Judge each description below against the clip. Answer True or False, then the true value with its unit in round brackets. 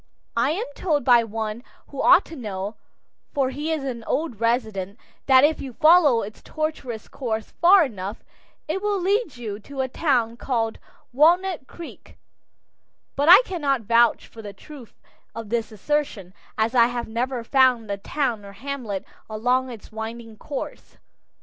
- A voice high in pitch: True (245 Hz)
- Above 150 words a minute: True (160 wpm)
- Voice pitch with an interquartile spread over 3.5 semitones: True (4.8 semitones)